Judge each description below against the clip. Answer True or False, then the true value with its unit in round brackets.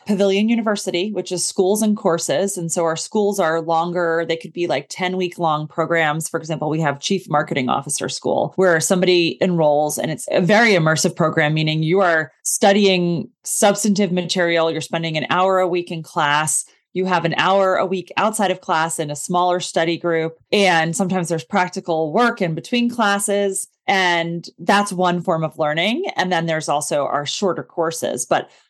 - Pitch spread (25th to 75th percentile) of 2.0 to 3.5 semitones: True (2.9 semitones)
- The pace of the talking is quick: False (185 wpm)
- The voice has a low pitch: False (175 Hz)